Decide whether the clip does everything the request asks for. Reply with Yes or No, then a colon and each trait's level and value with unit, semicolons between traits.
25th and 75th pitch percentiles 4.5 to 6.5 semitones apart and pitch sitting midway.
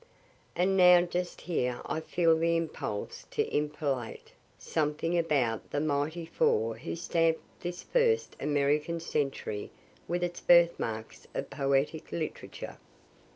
No: average, 3.5 semitones; medium, 160 Hz